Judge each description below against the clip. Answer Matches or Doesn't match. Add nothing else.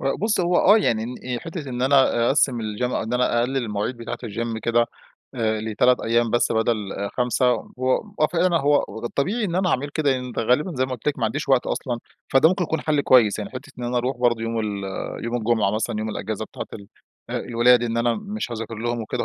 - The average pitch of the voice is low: Matches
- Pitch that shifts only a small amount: Doesn't match